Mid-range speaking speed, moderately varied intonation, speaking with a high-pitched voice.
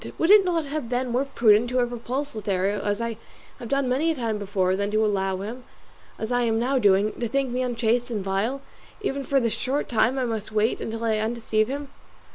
No: fast, 225 wpm; average, 3.4 semitones; high, 235 Hz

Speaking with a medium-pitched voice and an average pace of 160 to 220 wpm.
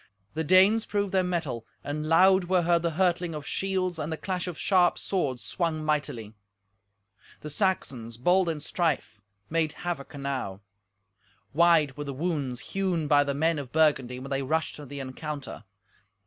Yes: medium, 155 Hz; average, 165 wpm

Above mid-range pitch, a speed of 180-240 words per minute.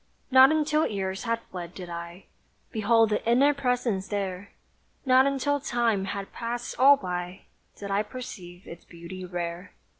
No: high, 205 Hz; average, 150 wpm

